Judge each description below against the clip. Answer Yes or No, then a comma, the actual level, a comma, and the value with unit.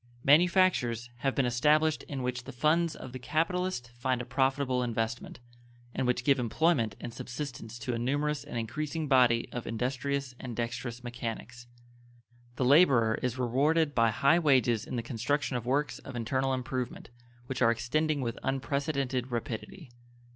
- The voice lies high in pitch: No, low, 130 Hz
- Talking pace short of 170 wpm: Yes, average, 155 wpm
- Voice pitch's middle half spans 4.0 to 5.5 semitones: No, average, 3.2 semitones